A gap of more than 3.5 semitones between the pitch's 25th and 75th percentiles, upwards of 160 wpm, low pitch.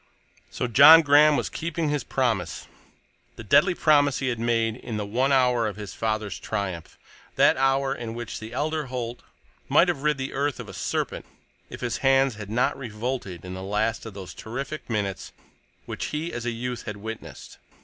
Yes: average, 4.1 semitones; average, 185 wpm; low, 120 Hz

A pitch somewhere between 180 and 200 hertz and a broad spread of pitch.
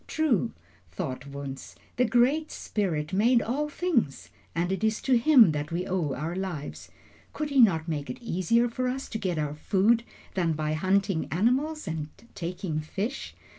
Yes: high, 190 Hz; wide, 7.4 semitones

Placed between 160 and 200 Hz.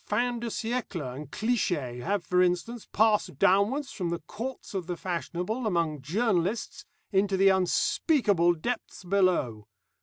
Yes: high, 190 Hz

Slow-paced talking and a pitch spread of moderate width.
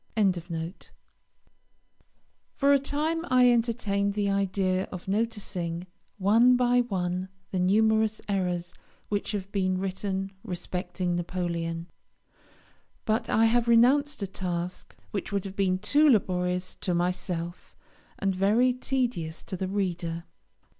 Yes: slow, 120 wpm; average, 3.9 semitones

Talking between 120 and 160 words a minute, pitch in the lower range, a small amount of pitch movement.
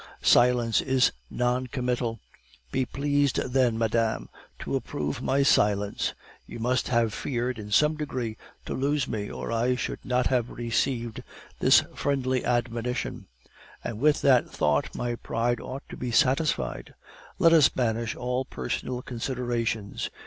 Yes: average, 140 wpm; low, 125 Hz; narrow, 2.2 semitones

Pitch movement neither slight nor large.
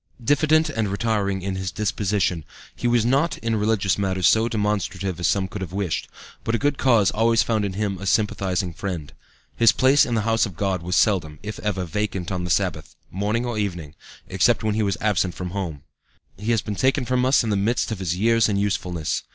Yes: average, 3.4 semitones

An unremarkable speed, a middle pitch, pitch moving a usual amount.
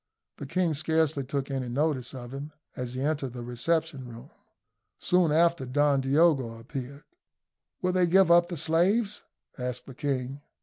Yes: average, 160 wpm; medium, 145 Hz; average, 4.2 semitones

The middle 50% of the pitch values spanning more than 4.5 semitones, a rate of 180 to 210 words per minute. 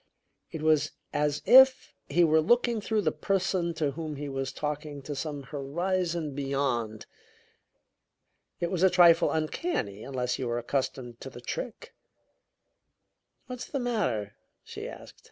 No: average, 5.1 semitones; average, 140 wpm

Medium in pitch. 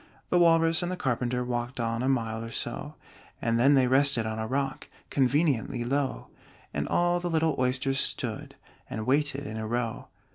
No: low, 130 Hz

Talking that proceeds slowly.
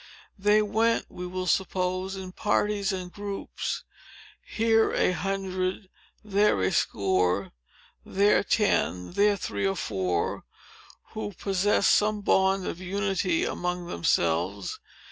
Yes: slow, 115 wpm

